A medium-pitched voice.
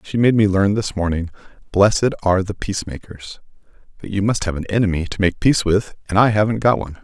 No: low, 100 Hz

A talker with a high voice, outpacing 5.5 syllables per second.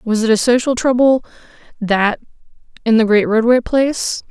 No: high, 235 Hz; 5.0 syllables/s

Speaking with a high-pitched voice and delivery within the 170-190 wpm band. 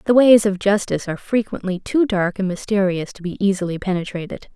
Yes: high, 195 Hz; average, 185 wpm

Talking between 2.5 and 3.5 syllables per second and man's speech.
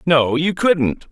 Yes: 3.0 syllables/s; male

